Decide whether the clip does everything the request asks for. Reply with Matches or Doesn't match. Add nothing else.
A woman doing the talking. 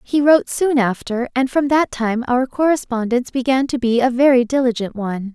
Matches